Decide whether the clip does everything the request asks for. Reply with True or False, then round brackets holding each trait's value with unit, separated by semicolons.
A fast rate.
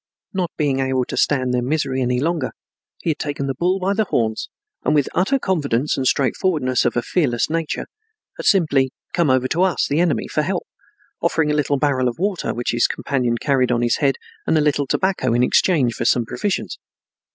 True (210 wpm)